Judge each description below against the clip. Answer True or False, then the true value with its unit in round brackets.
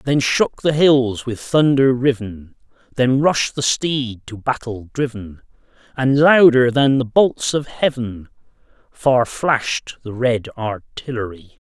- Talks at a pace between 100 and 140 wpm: True (135 wpm)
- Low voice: True (125 Hz)